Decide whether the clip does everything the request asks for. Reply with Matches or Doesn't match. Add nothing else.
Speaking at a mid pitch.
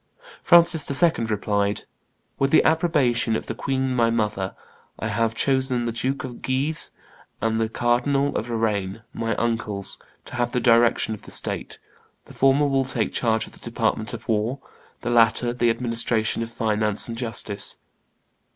Doesn't match